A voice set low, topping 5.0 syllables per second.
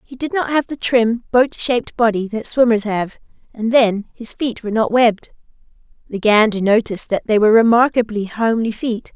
No: high, 230 Hz; 5.5 syllables/s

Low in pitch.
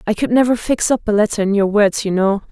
No: high, 210 Hz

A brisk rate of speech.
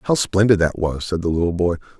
Yes: fast, 240 wpm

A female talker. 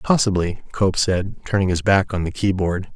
No: male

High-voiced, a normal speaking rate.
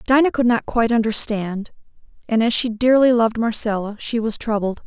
Yes: high, 230 Hz; average, 175 wpm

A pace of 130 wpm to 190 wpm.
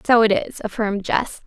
No: fast, 205 wpm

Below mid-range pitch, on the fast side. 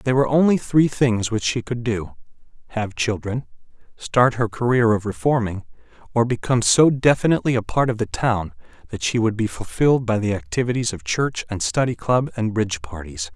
No: low, 115 Hz; average, 185 wpm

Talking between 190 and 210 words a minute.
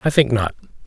Yes: fast, 205 wpm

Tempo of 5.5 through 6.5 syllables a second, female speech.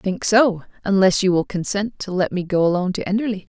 Yes: 6.2 syllables/s; female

